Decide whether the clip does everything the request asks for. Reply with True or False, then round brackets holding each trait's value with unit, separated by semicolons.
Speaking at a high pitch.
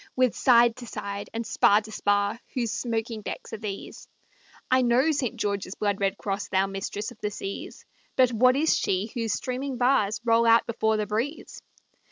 True (225 Hz)